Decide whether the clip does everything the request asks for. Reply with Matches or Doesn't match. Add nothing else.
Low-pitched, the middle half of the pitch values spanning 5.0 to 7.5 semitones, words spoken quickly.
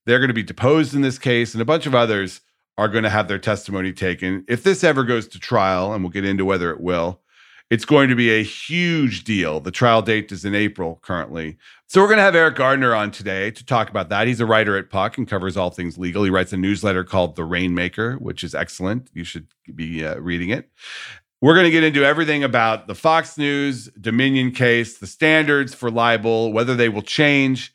Matches